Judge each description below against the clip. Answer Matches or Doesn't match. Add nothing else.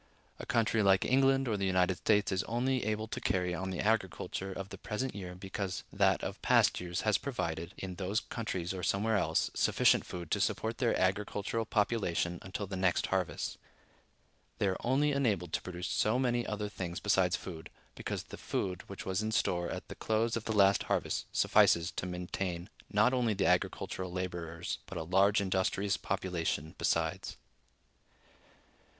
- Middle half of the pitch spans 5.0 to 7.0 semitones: Doesn't match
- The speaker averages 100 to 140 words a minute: Doesn't match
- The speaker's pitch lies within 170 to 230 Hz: Doesn't match